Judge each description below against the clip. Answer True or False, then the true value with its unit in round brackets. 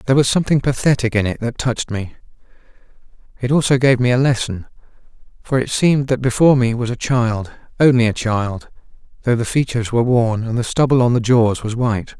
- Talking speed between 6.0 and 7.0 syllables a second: True (6.2 syllables/s)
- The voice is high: False (120 Hz)